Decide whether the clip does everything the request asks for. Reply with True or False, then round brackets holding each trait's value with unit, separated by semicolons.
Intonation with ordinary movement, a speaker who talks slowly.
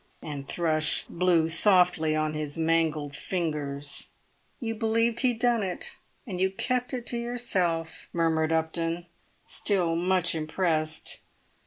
True (4.1 semitones; 130 wpm)